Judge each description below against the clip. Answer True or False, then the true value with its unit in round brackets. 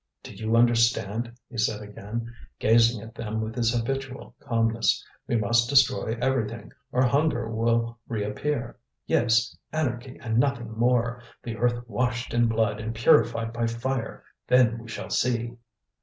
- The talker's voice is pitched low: True (115 Hz)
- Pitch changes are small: True (1.3 semitones)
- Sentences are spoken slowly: False (145 wpm)